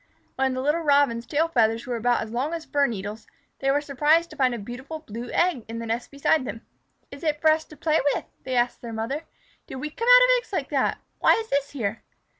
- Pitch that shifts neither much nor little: Yes, average, 4.7 semitones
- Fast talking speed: Yes, fast, 240 wpm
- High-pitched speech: Yes, very high, 275 Hz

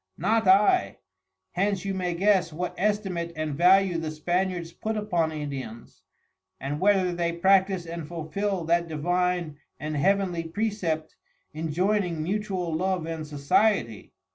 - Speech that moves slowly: Yes, slow, 130 wpm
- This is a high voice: No, medium, 175 Hz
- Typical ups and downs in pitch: Yes, average, 3.4 semitones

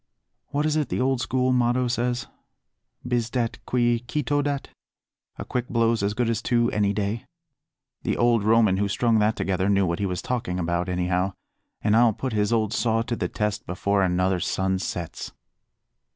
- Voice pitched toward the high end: No, low, 115 Hz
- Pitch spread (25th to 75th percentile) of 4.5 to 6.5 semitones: No, average, 3.7 semitones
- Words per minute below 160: No, average, 180 wpm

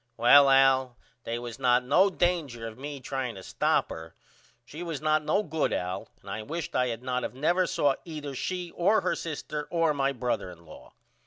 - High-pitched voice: No, medium, 140 Hz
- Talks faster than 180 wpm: Yes, average, 200 wpm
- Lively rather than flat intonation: No, average, 4.7 semitones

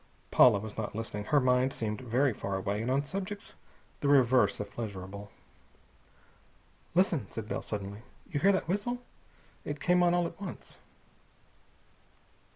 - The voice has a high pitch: No, low, 125 Hz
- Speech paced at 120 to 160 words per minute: Yes, average, 150 wpm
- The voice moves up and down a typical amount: No, wide, 8.8 semitones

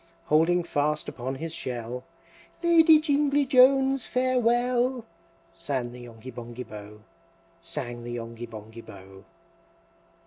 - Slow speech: Yes, slow, 110 wpm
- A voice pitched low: No, medium, 145 Hz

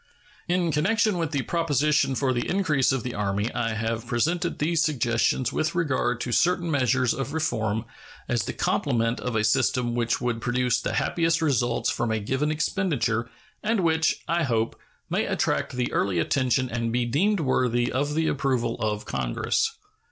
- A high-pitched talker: No, low, 130 Hz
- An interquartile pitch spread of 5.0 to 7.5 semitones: Yes, average, 5.3 semitones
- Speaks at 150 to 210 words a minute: Yes, average, 170 wpm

